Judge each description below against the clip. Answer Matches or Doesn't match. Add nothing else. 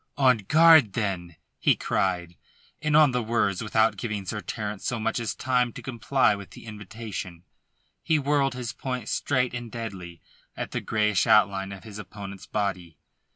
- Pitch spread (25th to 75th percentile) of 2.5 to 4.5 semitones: Matches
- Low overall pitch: Matches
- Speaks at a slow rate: Doesn't match